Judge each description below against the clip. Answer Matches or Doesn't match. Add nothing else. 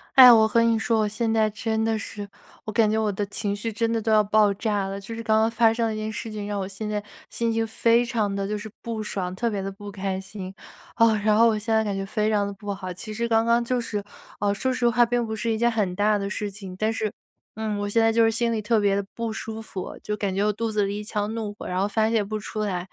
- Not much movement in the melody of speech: Matches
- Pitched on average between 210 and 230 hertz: Matches